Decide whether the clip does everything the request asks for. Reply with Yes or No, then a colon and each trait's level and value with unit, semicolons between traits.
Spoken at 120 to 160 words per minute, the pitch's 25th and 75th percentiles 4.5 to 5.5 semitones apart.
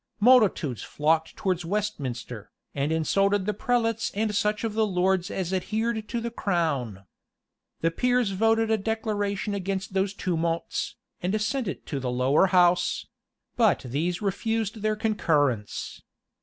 Yes: average, 140 wpm; average, 4.8 semitones